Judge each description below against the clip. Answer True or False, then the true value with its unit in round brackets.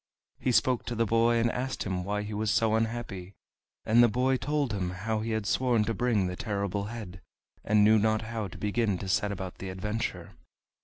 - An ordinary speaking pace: False (210 wpm)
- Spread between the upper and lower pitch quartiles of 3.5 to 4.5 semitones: False (2.6 semitones)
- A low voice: True (110 Hz)